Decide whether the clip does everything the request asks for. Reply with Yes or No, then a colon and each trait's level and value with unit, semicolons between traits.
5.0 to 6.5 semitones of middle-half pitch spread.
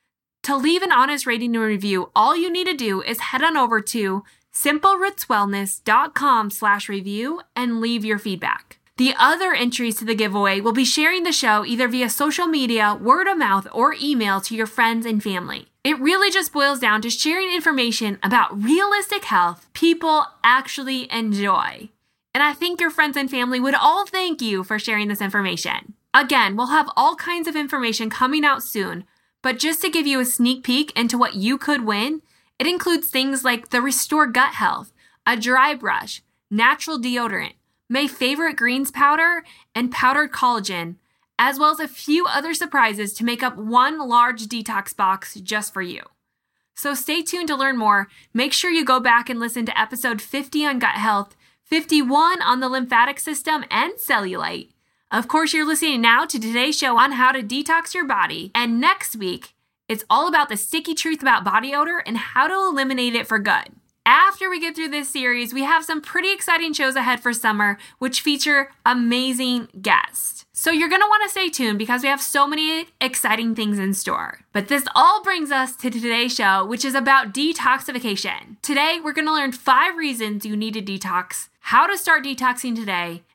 Yes: wide, 5.5 semitones